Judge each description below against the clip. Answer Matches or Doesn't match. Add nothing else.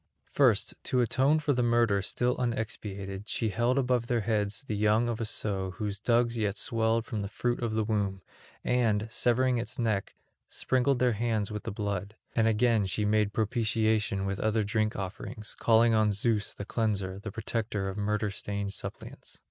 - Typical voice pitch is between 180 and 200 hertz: Doesn't match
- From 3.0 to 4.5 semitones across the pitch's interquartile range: Doesn't match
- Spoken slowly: Doesn't match